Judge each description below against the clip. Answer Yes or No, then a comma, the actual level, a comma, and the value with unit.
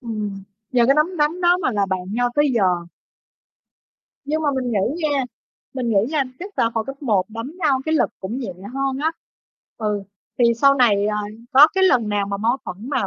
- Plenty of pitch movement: Yes, wide, 5.7 semitones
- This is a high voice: Yes, very high, 250 Hz